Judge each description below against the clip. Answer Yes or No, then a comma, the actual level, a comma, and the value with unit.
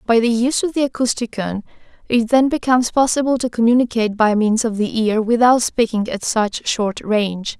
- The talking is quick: No, average, 180 wpm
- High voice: Yes, high, 230 Hz